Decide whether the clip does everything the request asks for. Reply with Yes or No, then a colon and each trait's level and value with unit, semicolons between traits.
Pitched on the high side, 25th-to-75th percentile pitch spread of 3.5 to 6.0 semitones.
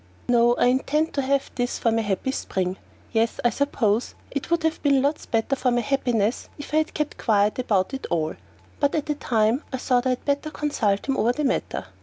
Yes: very high, 255 Hz; average, 4.0 semitones